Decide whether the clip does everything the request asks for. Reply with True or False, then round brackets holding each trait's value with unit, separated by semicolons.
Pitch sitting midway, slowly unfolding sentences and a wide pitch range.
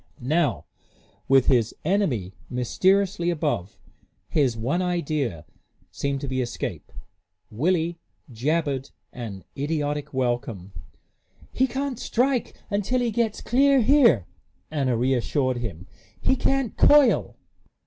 True (145 Hz; 105 wpm; 8.5 semitones)